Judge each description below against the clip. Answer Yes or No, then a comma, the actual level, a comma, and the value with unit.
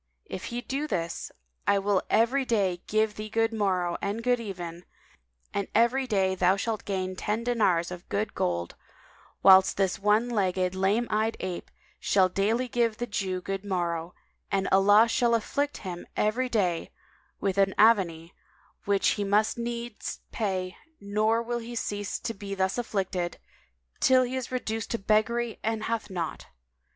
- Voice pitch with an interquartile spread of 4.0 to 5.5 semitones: No, average, 3.5 semitones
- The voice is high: Yes, high, 205 Hz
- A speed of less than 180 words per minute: Yes, average, 160 wpm